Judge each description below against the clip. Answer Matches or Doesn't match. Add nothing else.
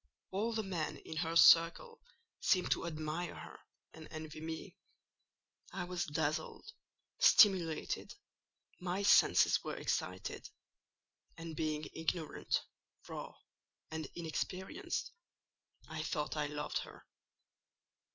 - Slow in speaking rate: Matches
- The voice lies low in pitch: Doesn't match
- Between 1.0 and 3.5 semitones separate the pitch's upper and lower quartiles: Matches